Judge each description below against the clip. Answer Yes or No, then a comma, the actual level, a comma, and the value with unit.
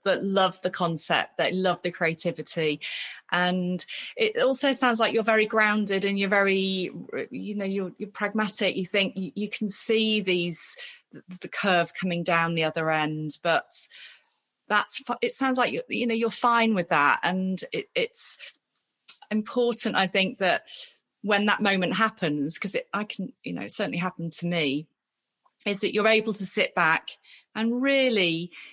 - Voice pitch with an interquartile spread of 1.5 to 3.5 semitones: No, average, 4.0 semitones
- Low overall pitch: No, high, 200 Hz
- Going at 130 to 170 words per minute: Yes, average, 165 wpm